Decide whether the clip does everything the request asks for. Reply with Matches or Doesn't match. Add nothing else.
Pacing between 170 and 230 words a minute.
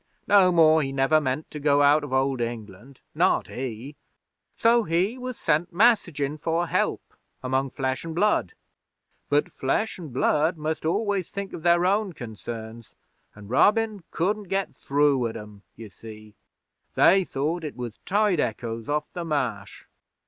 Doesn't match